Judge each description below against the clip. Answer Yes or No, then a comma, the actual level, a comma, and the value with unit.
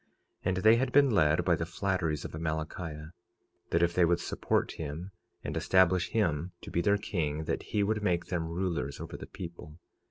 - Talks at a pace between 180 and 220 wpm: Yes, average, 195 wpm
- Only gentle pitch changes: No, average, 3.0 semitones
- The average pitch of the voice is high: No, very low, 85 Hz